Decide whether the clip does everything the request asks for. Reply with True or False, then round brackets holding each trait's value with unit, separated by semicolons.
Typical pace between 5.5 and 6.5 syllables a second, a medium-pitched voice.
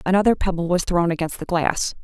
True (5.9 syllables/s; 175 Hz)